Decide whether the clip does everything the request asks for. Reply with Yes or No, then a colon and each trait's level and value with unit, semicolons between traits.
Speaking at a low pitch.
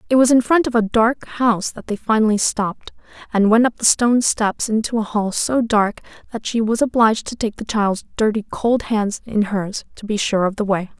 No: high, 220 Hz